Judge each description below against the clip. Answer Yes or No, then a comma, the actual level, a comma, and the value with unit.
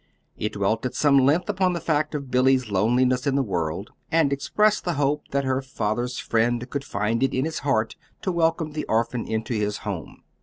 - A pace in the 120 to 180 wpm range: No, average, 200 wpm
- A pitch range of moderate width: Yes, average, 4.7 semitones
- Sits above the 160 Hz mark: No, low, 130 Hz